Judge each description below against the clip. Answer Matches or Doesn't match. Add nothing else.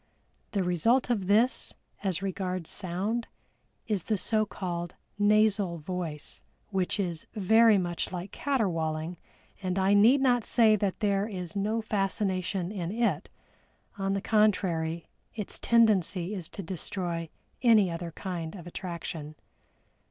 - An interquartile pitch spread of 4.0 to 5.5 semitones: Doesn't match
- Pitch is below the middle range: Doesn't match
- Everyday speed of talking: Doesn't match